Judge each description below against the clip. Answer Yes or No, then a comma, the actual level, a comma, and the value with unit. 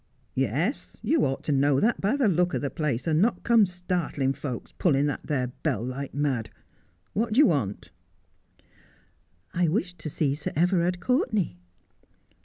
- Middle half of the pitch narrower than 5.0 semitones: No, wide, 5.6 semitones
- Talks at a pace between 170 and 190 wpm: Yes, average, 180 wpm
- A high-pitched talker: No, medium, 155 Hz